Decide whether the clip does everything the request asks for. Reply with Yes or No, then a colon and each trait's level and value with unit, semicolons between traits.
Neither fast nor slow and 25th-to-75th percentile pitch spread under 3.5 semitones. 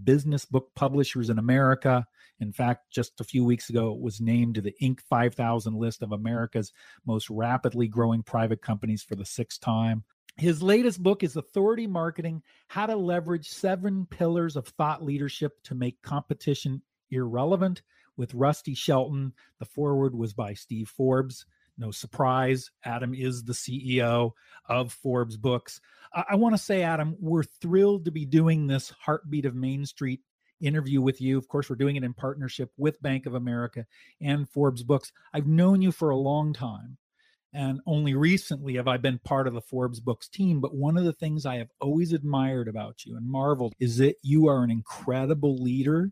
No: average, 180 wpm; average, 4.1 semitones